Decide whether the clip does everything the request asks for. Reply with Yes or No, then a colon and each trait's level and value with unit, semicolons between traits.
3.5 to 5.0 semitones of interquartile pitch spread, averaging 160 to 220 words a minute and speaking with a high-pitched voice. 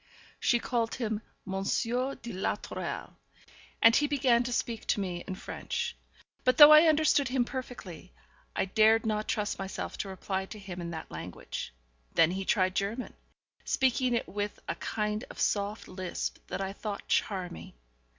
Yes: average, 4.2 semitones; average, 165 wpm; high, 210 Hz